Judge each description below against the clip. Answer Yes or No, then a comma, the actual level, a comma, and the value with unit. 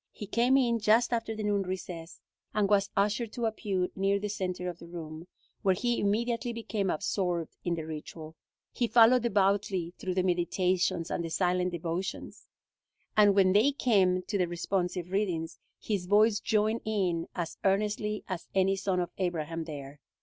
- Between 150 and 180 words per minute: Yes, average, 170 wpm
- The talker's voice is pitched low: No, high, 190 Hz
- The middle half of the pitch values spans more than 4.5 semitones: No, average, 3.2 semitones